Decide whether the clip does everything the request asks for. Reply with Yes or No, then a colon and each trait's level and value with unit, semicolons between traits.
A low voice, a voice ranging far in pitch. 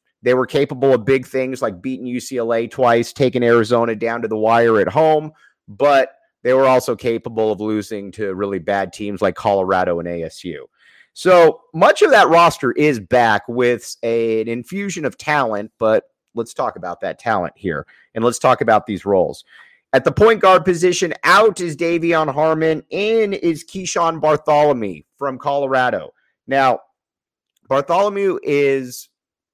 Yes: low, 130 Hz; wide, 5.8 semitones